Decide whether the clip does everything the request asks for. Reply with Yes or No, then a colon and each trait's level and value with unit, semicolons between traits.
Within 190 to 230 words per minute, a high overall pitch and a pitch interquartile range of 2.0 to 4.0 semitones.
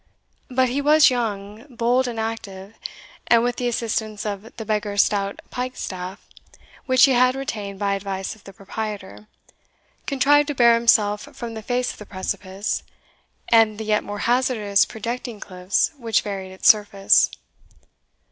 No: average, 155 wpm; high, 220 Hz; average, 3.4 semitones